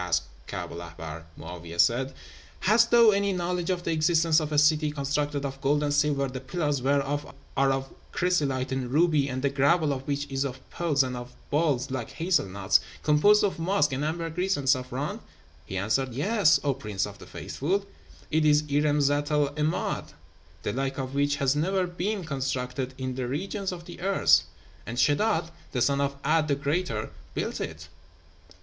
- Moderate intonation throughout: Yes, average, 3.9 semitones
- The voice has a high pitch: No, medium, 145 Hz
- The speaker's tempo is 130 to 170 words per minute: No, average, 185 wpm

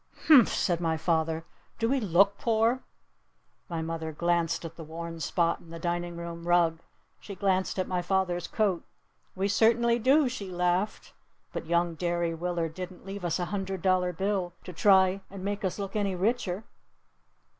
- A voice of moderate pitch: Yes, medium, 180 Hz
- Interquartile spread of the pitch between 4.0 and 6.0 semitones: No, average, 2.9 semitones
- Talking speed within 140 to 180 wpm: Yes, average, 170 wpm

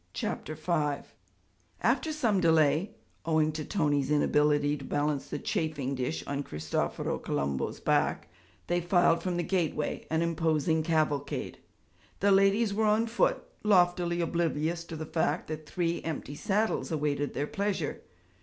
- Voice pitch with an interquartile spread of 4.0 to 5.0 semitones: No, average, 3.5 semitones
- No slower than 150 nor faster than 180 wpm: No, average, 140 wpm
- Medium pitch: Yes, medium, 160 Hz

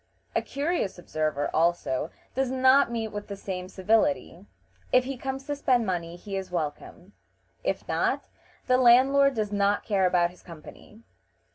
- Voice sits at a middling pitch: No, high, 205 Hz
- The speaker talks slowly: No, average, 155 wpm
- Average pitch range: No, wide, 6.4 semitones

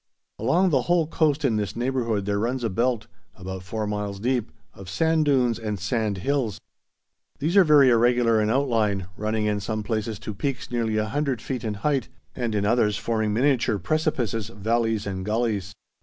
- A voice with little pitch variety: No, average, 3.8 semitones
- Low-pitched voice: Yes, low, 115 Hz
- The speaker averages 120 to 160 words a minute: No, average, 175 wpm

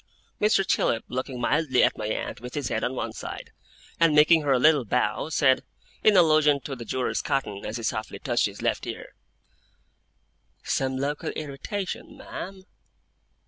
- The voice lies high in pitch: No, low, 135 Hz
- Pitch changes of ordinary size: Yes, average, 4.0 semitones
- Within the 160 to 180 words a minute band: Yes, average, 165 wpm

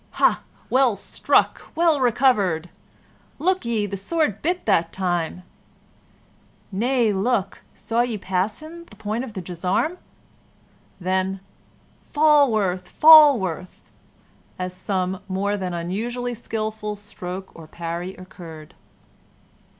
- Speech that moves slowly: Yes, slow, 110 wpm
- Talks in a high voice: Yes, high, 205 Hz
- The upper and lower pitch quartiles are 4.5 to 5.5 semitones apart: Yes, average, 5.1 semitones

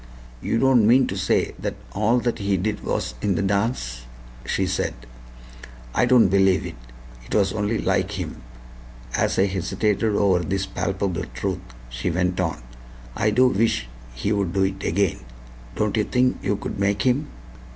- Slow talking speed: No, average, 165 wpm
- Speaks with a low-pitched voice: Yes, low, 100 Hz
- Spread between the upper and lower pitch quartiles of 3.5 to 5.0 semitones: No, narrow, 2.6 semitones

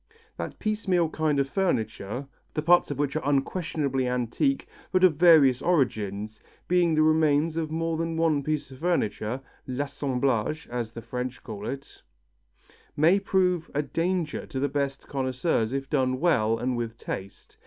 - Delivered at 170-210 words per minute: No, average, 155 wpm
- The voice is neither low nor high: Yes, medium, 145 Hz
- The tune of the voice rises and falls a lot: No, average, 4.7 semitones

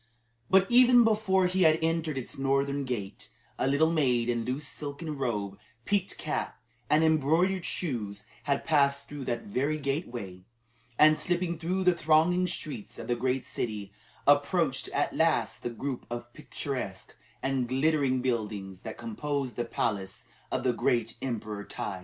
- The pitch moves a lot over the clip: No, average, 5.0 semitones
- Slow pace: No, average, 150 wpm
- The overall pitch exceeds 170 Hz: No, medium, 140 Hz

